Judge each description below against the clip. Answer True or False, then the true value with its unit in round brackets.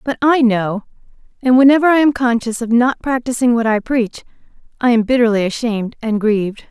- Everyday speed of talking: True (180 wpm)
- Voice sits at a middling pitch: False (235 Hz)